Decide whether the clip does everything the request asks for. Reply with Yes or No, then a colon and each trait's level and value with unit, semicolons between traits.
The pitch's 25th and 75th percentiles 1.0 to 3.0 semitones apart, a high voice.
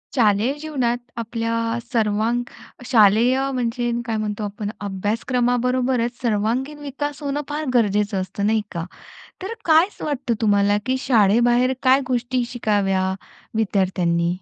No: average, 3.8 semitones; high, 235 Hz